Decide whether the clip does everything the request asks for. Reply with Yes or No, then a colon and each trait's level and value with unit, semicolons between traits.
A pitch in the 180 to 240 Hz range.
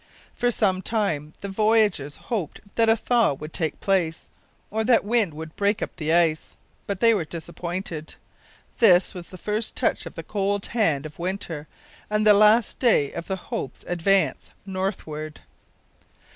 Yes: high, 190 Hz